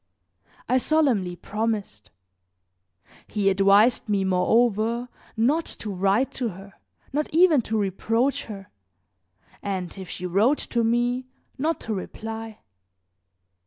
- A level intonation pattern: No, average, 4.0 semitones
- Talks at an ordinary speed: No, slow, 115 wpm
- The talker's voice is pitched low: No, high, 220 Hz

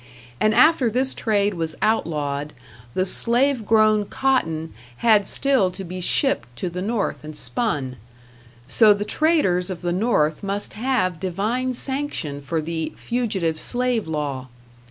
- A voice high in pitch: Yes, high, 200 Hz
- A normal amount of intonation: No, wide, 6.6 semitones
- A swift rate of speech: No, average, 140 wpm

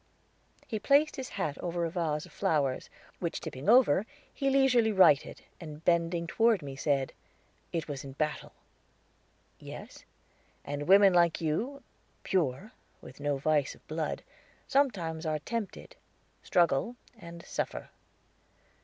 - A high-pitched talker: No, medium, 170 Hz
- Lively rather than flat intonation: Yes, wide, 6.2 semitones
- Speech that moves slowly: Yes, slow, 130 wpm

